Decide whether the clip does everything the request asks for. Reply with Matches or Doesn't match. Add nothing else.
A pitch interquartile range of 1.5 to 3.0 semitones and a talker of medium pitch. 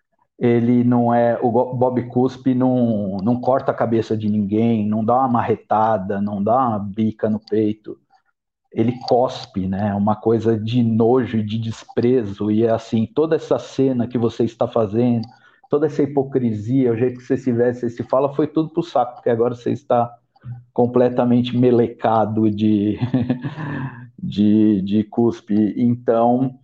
Doesn't match